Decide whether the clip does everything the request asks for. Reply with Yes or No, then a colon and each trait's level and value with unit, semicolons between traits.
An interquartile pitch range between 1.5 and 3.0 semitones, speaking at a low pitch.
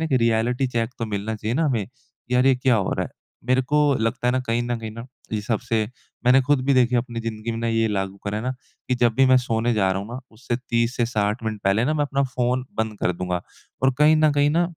Yes: average, 2.7 semitones; low, 120 Hz